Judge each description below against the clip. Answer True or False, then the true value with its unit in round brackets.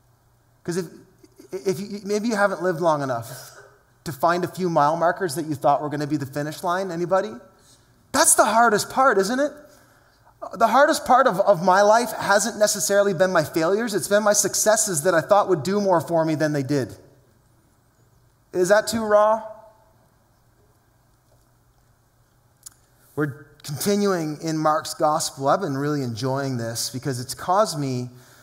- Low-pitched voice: False (160 Hz)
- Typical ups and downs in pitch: False (8.2 semitones)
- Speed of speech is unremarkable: True (165 wpm)